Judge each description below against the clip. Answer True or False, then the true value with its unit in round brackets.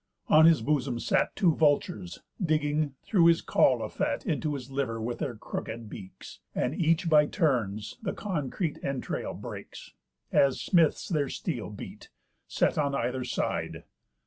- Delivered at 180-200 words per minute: False (150 wpm)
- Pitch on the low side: False (145 Hz)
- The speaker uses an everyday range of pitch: True (4.5 semitones)